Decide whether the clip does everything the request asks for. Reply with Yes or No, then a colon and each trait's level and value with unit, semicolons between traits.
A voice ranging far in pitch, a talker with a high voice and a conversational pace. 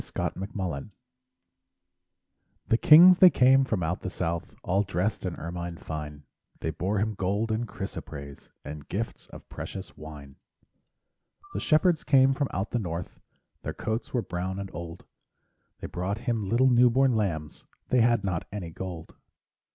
No: wide, 5.7 semitones; very low, 95 Hz; average, 155 wpm